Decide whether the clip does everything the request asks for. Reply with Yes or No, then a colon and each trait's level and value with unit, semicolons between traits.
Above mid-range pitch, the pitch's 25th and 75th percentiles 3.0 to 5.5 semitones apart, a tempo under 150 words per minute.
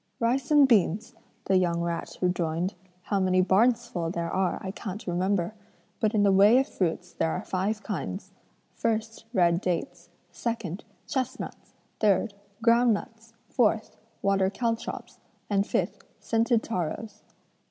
Yes: high, 200 Hz; average, 4.0 semitones; average, 140 wpm